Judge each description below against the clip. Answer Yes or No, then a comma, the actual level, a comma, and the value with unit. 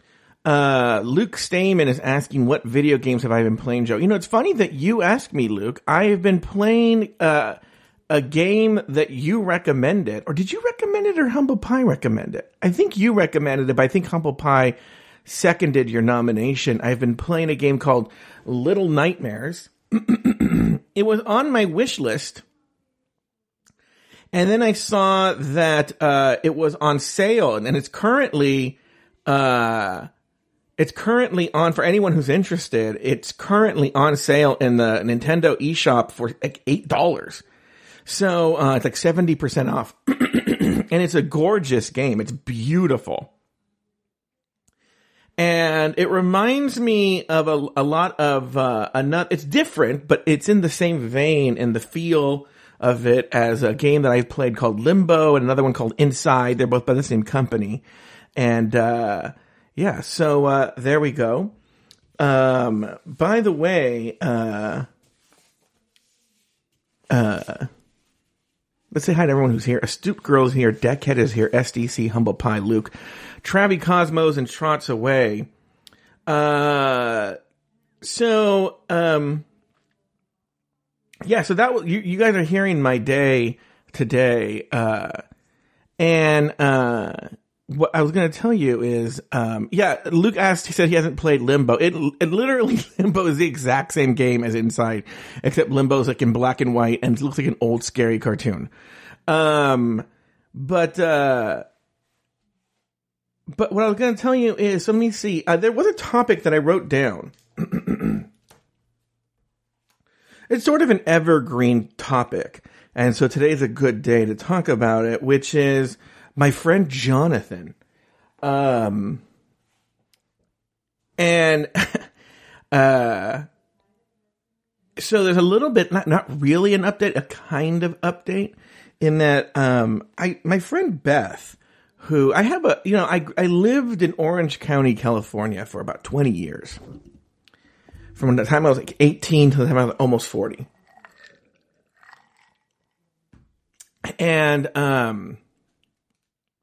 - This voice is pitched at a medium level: Yes, medium, 150 Hz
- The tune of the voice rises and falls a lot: Yes, wide, 6.5 semitones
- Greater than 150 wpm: No, average, 145 wpm